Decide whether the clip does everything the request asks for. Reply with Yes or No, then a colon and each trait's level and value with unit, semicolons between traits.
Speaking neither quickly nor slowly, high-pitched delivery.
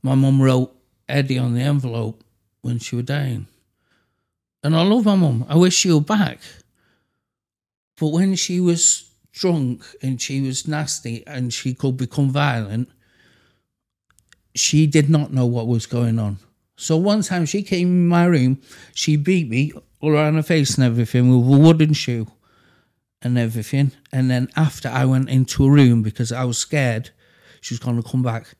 No: average, 175 wpm; low, 130 Hz